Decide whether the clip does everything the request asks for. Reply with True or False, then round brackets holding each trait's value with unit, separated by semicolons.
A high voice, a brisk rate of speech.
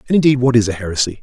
False (120 Hz; 295 wpm)